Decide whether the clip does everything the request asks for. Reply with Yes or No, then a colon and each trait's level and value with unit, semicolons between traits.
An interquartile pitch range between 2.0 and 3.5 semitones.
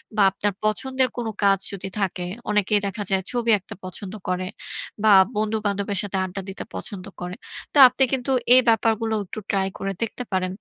Yes: average, 2.7 semitones